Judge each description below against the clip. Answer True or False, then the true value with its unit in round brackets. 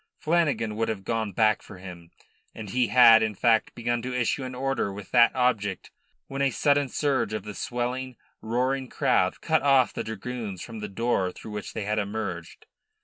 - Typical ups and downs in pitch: True (3.4 semitones)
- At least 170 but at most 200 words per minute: True (190 wpm)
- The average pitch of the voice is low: True (115 Hz)